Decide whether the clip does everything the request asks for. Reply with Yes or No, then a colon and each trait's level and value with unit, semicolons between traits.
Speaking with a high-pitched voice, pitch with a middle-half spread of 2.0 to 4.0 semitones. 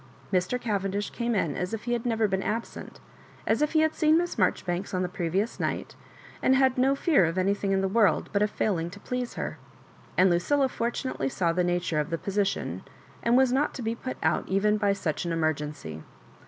No: high, 200 Hz; average, 5.2 semitones